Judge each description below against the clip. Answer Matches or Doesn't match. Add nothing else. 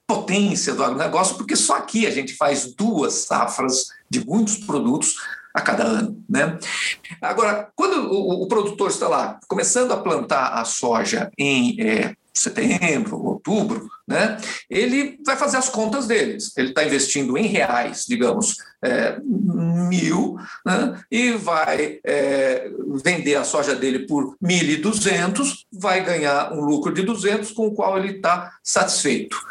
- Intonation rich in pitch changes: Matches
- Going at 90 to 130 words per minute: Doesn't match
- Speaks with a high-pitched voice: Matches